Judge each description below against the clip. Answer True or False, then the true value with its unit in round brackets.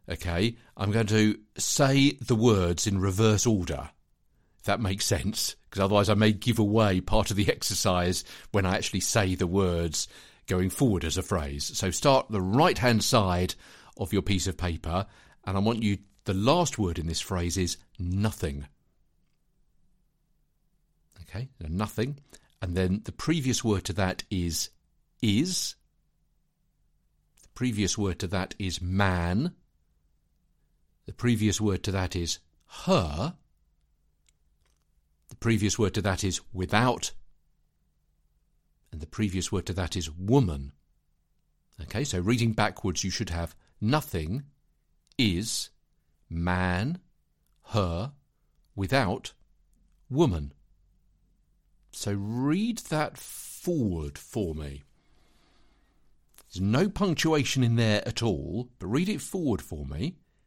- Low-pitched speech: True (100 Hz)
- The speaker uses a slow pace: True (130 wpm)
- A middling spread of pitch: True (4.5 semitones)